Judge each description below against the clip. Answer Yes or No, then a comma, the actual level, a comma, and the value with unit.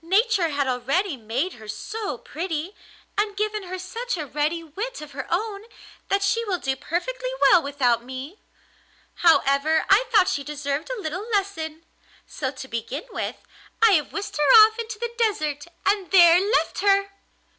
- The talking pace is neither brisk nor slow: Yes, average, 165 wpm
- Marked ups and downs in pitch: Yes, wide, 6.3 semitones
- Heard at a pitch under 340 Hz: No, very high, 345 Hz